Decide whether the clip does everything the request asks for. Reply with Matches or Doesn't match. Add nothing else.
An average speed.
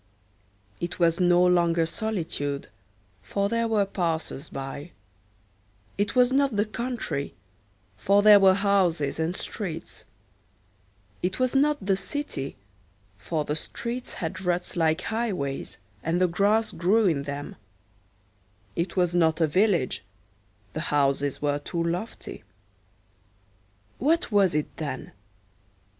Doesn't match